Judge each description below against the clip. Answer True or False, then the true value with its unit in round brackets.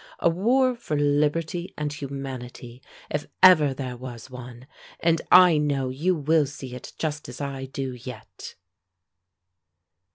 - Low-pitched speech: False (145 Hz)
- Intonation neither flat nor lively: True (3.9 semitones)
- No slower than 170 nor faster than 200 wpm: False (135 wpm)